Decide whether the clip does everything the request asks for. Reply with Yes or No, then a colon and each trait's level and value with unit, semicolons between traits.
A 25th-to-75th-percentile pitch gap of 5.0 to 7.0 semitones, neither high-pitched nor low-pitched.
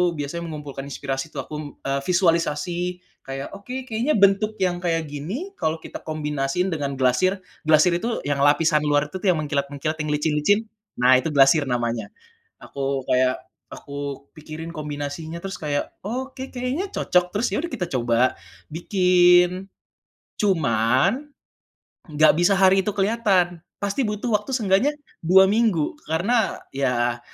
Yes: wide, 5.4 semitones; medium, 165 Hz